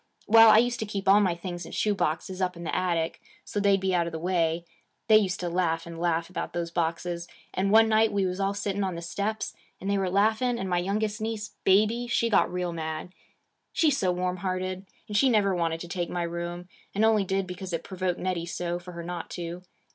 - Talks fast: Yes, fast, 240 wpm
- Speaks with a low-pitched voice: No, medium, 185 Hz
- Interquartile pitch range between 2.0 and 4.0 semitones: Yes, average, 2.8 semitones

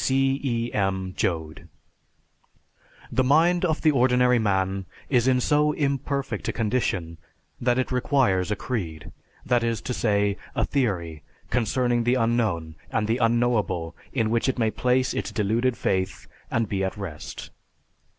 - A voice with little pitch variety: No, average, 4.8 semitones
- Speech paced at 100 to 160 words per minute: Yes, average, 150 wpm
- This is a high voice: No, low, 115 Hz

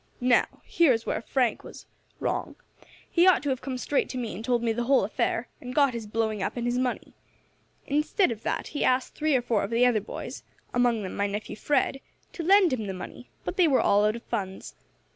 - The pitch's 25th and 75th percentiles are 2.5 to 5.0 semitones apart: Yes, average, 3.8 semitones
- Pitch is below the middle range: No, high, 245 Hz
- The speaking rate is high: Yes, fast, 230 wpm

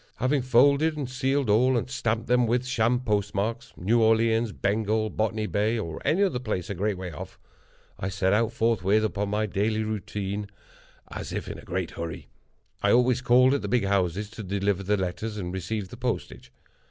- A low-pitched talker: Yes, low, 110 Hz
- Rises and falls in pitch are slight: No, average, 3.4 semitones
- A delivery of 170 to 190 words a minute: Yes, average, 185 wpm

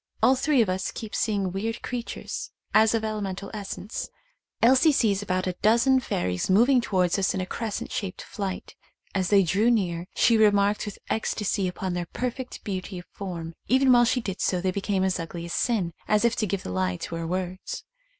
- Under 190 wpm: No, average, 200 wpm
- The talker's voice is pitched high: Yes, high, 200 Hz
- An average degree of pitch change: Yes, average, 3.7 semitones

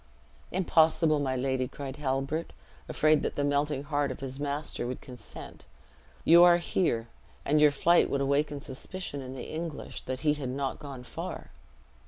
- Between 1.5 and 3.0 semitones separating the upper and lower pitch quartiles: Yes, narrow, 2.5 semitones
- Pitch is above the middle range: No, medium, 145 Hz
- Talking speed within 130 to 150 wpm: No, average, 170 wpm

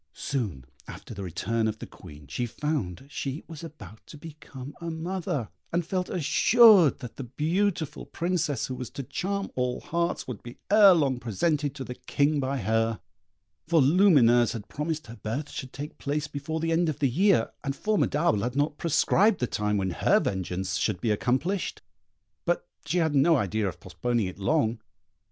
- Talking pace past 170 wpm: Yes, average, 180 wpm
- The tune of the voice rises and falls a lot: Yes, wide, 6.2 semitones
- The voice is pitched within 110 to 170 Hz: Yes, medium, 140 Hz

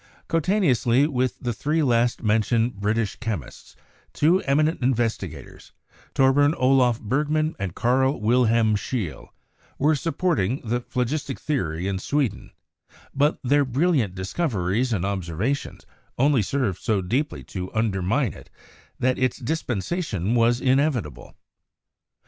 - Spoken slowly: Yes, slow, 120 wpm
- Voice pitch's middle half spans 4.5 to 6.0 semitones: Yes, average, 5.2 semitones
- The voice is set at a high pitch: No, low, 125 Hz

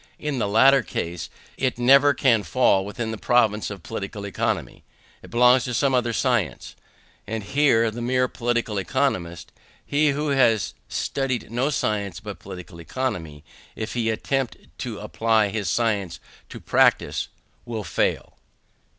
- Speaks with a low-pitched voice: Yes, low, 115 Hz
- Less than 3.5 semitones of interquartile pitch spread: No, average, 4.2 semitones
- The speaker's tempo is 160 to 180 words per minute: No, average, 145 wpm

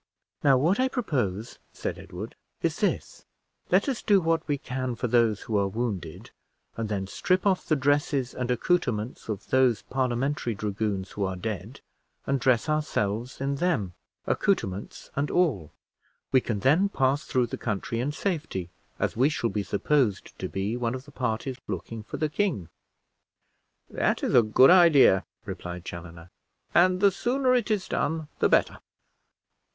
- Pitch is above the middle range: No, low, 125 Hz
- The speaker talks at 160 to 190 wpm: Yes, average, 165 wpm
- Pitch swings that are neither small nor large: No, wide, 6.6 semitones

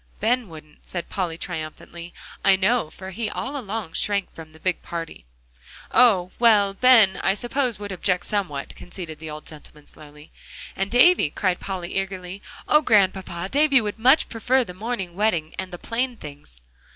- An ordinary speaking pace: Yes, average, 165 wpm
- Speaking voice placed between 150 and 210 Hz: Yes, high, 190 Hz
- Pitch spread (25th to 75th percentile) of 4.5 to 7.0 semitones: Yes, average, 5.0 semitones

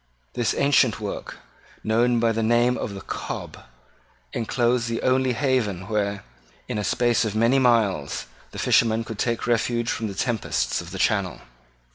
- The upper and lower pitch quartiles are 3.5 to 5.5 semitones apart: No, narrow, 2.6 semitones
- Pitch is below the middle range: Yes, low, 115 Hz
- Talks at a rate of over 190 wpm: No, average, 160 wpm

